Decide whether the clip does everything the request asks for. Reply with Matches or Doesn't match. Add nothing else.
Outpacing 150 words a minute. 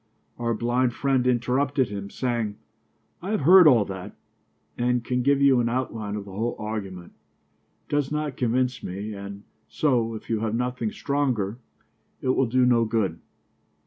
Matches